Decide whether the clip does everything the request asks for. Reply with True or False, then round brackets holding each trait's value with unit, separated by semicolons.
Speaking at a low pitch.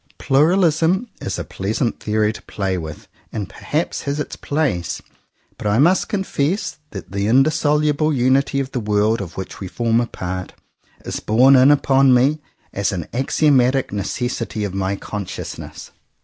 True (125 Hz)